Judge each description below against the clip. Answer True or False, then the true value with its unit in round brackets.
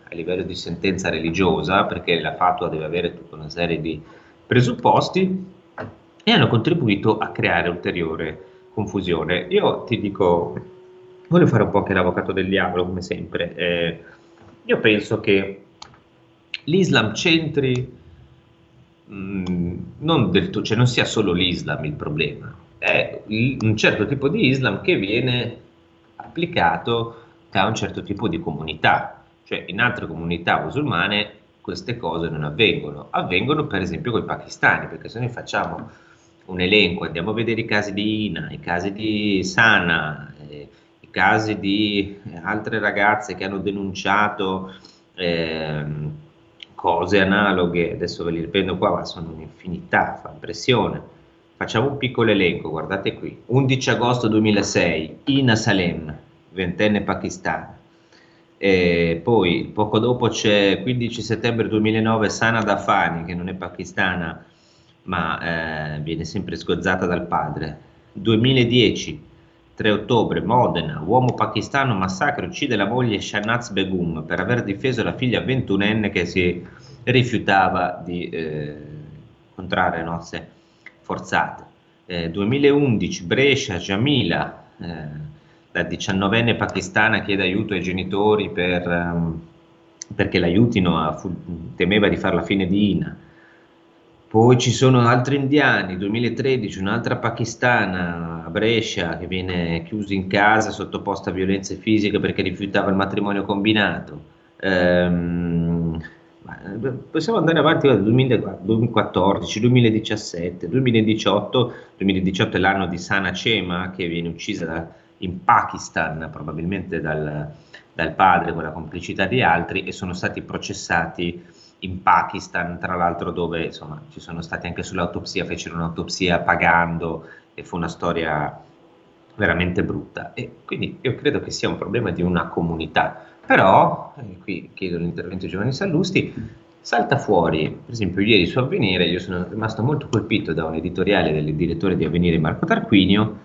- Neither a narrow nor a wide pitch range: True (4.2 semitones)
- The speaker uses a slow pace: False (135 wpm)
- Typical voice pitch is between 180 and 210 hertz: False (95 Hz)